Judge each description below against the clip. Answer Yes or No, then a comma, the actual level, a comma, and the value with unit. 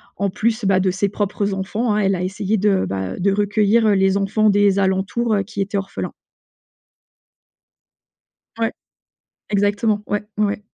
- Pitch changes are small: Yes, narrow, 1.5 semitones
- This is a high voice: Yes, high, 200 Hz